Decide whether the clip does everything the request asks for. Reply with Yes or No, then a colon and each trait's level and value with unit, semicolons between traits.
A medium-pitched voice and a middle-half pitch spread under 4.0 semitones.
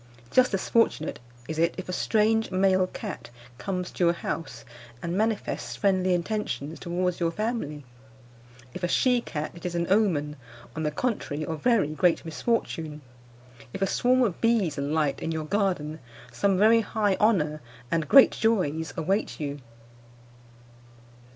No: medium, 180 Hz; average, 5.1 semitones